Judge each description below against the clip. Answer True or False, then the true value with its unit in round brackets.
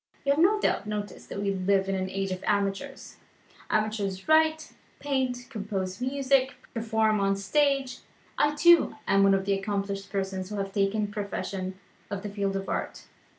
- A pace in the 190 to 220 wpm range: False (175 wpm)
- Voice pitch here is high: True (205 Hz)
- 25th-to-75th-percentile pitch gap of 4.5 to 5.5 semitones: True (4.9 semitones)